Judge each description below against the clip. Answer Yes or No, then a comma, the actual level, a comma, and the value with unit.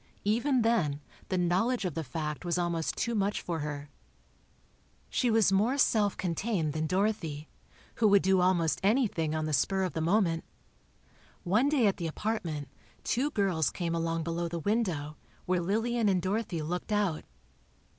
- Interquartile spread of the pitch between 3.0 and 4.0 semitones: No, average, 4.7 semitones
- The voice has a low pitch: No, medium, 185 Hz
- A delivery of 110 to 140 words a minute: No, average, 165 wpm